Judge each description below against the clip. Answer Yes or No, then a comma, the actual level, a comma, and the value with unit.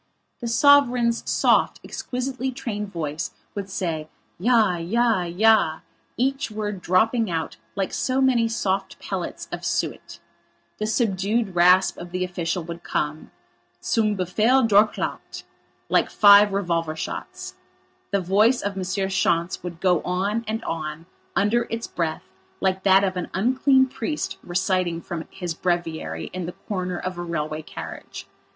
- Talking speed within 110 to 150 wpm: Yes, average, 140 wpm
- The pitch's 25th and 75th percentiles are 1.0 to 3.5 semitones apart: No, average, 4.5 semitones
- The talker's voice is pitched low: No, high, 190 Hz